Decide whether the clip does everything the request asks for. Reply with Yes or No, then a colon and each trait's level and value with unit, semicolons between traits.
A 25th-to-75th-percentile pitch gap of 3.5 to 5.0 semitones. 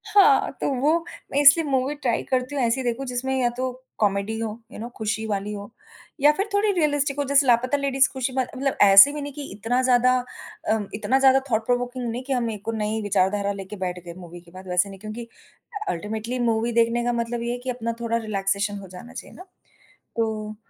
Yes: average, 4.1 semitones